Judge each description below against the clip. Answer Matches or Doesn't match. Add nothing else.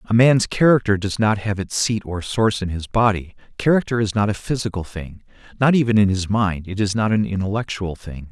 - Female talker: Doesn't match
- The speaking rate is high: Matches